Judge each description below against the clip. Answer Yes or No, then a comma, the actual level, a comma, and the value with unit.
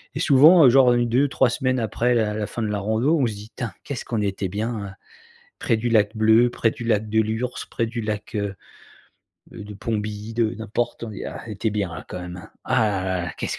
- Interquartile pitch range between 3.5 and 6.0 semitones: No, narrow, 2.5 semitones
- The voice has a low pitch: Yes, low, 110 Hz